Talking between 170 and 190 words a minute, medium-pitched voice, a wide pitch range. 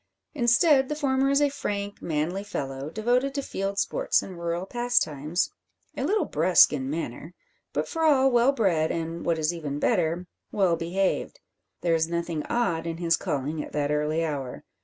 Yes: average, 175 wpm; medium, 175 Hz; wide, 7.2 semitones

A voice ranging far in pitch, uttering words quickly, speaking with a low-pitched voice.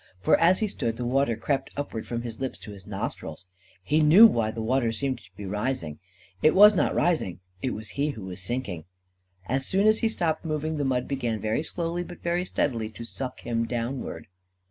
Yes: wide, 5.9 semitones; fast, 210 wpm; low, 130 Hz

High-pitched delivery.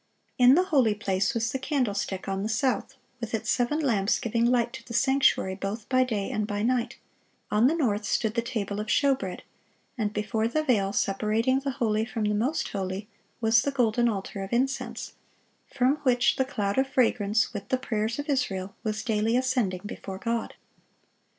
Yes: high, 230 Hz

